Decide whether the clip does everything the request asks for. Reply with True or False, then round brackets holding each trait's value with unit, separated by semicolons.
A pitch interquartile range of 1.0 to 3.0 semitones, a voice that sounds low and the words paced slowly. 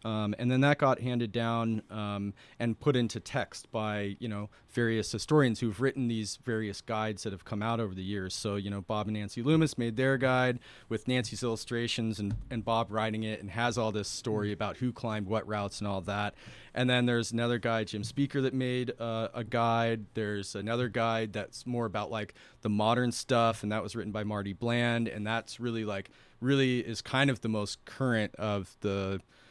False (2.4 semitones; 115 Hz; 205 wpm)